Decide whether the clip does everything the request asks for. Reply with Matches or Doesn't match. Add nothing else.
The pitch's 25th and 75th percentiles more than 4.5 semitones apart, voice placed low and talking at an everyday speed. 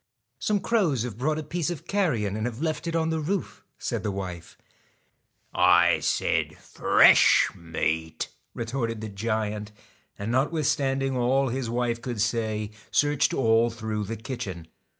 Matches